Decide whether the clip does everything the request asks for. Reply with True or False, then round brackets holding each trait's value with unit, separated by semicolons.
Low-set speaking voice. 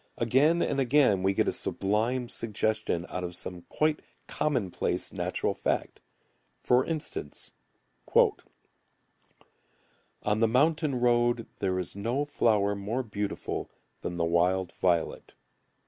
True (110 Hz)